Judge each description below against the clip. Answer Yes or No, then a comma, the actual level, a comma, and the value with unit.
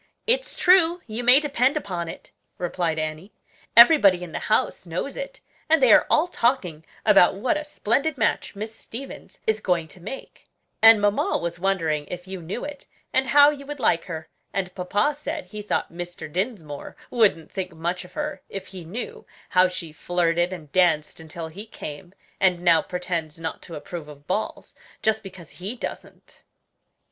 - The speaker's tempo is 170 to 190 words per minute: Yes, average, 175 wpm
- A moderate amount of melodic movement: No, wide, 6.3 semitones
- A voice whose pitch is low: No, high, 190 Hz